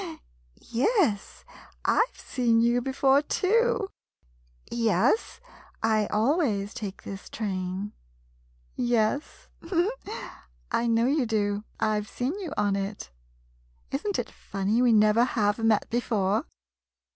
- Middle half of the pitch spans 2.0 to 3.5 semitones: No, average, 4.5 semitones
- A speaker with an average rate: No, slow, 120 wpm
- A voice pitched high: Yes, high, 230 Hz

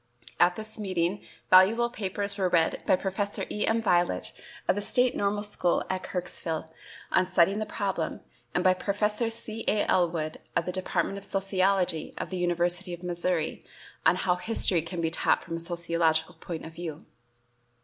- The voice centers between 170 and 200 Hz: Yes, medium, 185 Hz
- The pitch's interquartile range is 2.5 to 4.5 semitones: Yes, average, 2.9 semitones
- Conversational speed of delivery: Yes, average, 170 wpm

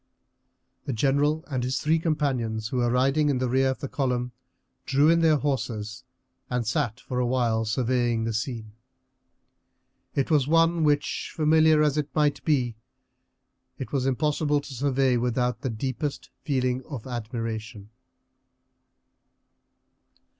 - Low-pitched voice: Yes, low, 130 Hz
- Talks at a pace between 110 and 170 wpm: Yes, average, 140 wpm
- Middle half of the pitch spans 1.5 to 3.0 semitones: No, average, 3.5 semitones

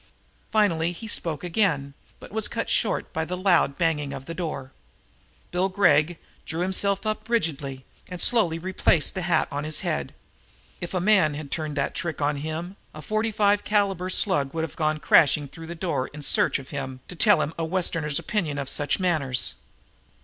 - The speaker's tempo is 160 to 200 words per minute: Yes, average, 185 wpm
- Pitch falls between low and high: Yes, medium, 165 Hz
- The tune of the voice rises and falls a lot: No, average, 4.4 semitones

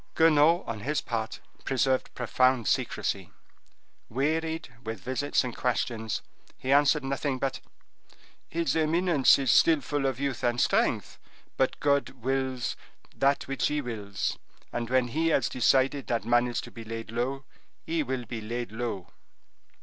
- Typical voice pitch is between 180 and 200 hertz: No, low, 130 Hz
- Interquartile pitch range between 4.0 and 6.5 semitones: No, average, 3.2 semitones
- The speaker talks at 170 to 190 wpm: No, average, 150 wpm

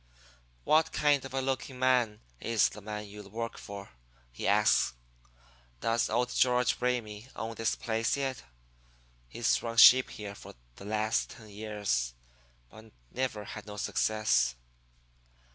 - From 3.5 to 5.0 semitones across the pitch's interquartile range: No, average, 3.0 semitones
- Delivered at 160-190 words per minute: No, average, 140 wpm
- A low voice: Yes, low, 110 Hz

